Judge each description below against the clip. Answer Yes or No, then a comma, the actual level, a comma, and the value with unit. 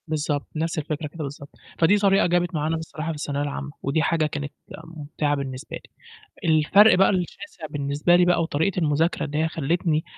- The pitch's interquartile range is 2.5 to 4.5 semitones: Yes, average, 2.8 semitones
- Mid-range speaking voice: Yes, medium, 155 Hz